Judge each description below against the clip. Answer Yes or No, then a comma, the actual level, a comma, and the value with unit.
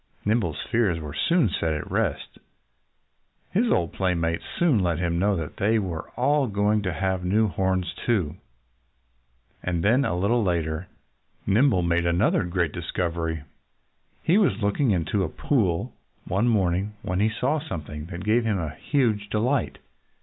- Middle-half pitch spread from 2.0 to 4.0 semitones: No, average, 4.7 semitones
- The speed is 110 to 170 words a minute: Yes, average, 150 wpm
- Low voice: Yes, very low, 95 Hz